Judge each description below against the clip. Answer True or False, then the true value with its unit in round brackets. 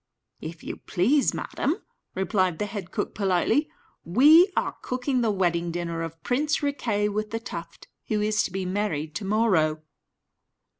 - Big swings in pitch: True (5.7 semitones)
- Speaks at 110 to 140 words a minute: False (155 wpm)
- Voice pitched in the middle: False (205 Hz)